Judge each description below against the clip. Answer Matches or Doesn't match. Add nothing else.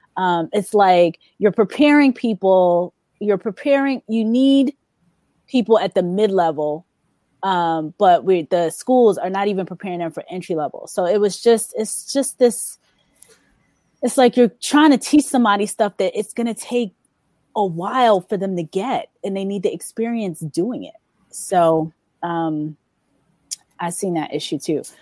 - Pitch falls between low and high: Doesn't match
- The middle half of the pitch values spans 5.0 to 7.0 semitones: Matches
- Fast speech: Doesn't match